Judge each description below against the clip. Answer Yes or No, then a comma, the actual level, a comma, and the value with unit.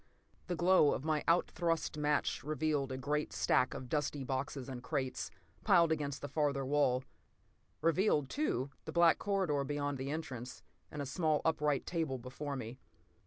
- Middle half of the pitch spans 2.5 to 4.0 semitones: Yes, average, 3.0 semitones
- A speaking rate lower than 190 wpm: Yes, average, 165 wpm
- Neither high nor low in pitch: Yes, medium, 145 Hz